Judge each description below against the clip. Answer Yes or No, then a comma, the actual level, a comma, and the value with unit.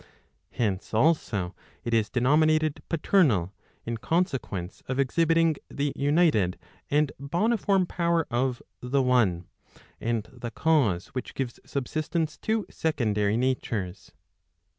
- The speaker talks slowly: Yes, slow, 110 wpm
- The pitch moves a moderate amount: No, wide, 6.1 semitones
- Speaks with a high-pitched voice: No, low, 135 Hz